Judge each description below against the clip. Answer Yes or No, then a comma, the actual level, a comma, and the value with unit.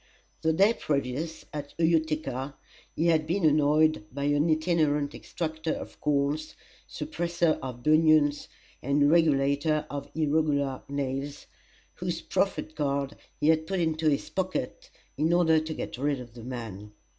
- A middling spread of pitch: No, narrow, 2.2 semitones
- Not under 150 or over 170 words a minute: No, average, 140 wpm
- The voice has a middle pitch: Yes, medium, 150 Hz